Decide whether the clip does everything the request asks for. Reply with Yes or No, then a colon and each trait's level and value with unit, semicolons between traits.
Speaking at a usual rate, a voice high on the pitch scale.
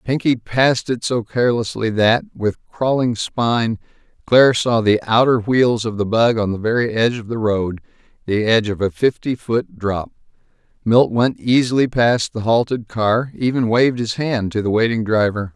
No: average, 170 wpm; low, 115 Hz